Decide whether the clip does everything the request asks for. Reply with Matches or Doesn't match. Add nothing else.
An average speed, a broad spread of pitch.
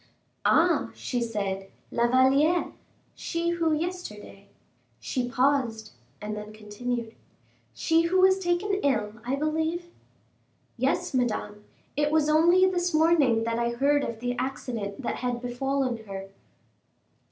Doesn't match